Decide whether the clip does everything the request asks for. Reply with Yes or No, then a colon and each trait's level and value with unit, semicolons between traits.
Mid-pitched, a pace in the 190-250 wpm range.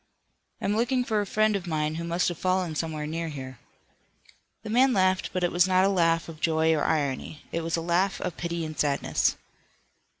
Yes: medium, 170 Hz; fast, 205 wpm